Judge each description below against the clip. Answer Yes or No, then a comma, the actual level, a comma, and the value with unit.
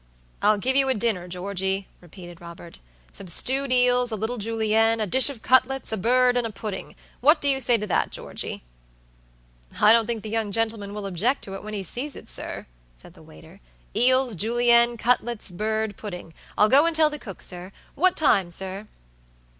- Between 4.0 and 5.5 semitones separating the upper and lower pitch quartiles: Yes, average, 4.3 semitones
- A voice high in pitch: Yes, high, 220 Hz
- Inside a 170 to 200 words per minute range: Yes, average, 185 wpm